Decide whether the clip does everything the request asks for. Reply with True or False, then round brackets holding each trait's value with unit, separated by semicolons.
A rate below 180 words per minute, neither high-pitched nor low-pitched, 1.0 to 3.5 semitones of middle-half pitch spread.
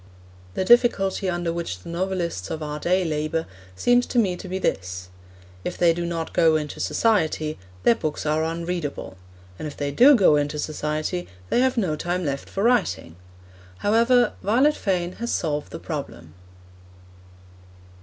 False (160 wpm; 170 Hz; 4.2 semitones)